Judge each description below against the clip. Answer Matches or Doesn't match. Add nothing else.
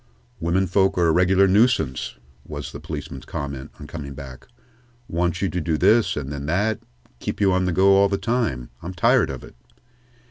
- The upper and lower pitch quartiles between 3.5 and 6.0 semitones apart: Matches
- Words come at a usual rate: Matches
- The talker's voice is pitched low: Matches